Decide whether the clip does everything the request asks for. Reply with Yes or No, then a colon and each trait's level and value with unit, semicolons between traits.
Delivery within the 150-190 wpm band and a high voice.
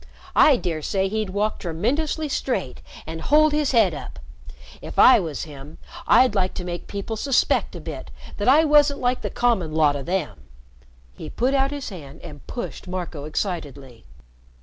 Yes: average, 170 wpm; high, 195 Hz